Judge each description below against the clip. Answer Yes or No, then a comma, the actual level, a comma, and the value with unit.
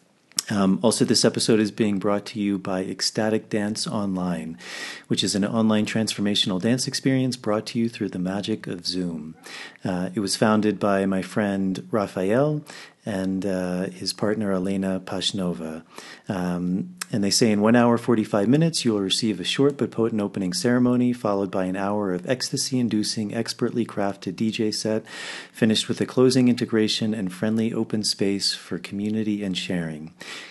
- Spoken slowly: No, average, 165 wpm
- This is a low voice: Yes, low, 105 Hz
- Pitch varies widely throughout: No, average, 3.2 semitones